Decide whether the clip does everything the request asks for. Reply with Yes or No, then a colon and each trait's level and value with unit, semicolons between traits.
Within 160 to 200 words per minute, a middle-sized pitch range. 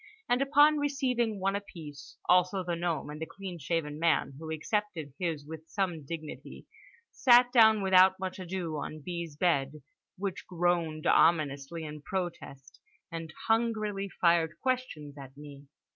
No: slow, 135 wpm; average, 4.4 semitones